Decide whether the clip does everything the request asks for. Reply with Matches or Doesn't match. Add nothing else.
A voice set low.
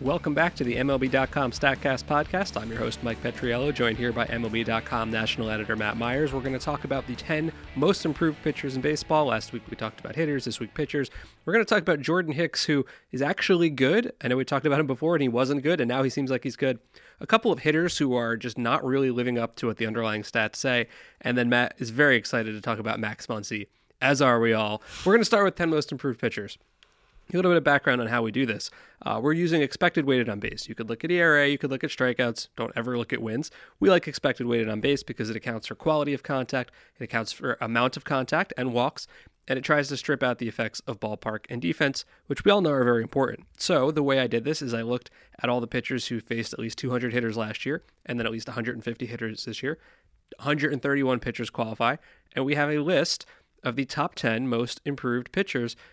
Matches